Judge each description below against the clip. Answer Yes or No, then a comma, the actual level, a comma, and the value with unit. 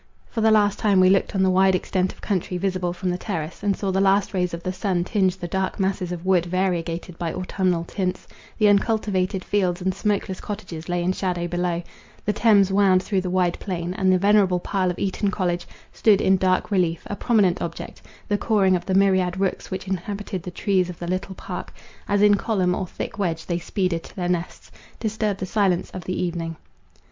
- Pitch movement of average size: No, narrow, 1.9 semitones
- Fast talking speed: Yes, fast, 210 wpm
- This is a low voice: No, medium, 185 Hz